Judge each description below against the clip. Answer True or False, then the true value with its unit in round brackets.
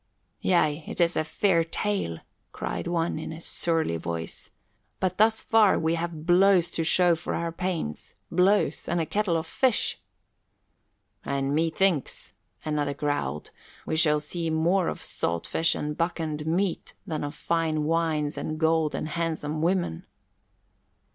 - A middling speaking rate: True (150 wpm)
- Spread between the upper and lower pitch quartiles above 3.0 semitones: False (2.4 semitones)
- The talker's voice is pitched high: False (165 Hz)